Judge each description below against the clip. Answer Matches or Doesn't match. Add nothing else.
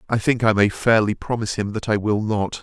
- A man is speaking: Matches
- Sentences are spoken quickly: Matches